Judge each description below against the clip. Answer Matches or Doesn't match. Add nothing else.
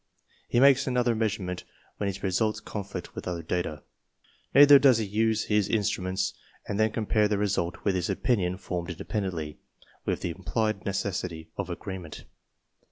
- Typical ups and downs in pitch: Matches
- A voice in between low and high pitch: Doesn't match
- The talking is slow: Doesn't match